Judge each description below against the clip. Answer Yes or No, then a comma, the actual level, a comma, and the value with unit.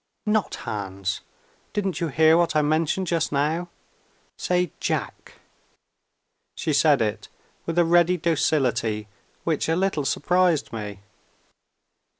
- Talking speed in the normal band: No, slow, 120 wpm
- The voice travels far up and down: No, average, 4.4 semitones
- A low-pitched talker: No, medium, 160 Hz